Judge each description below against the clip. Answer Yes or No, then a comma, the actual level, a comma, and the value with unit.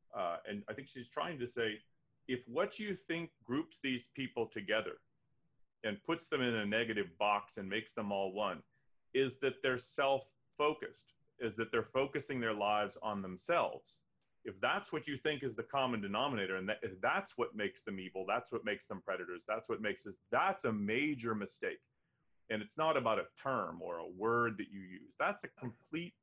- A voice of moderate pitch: No, low, 125 Hz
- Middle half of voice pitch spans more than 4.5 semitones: Yes, wide, 5.5 semitones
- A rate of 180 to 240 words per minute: Yes, average, 195 wpm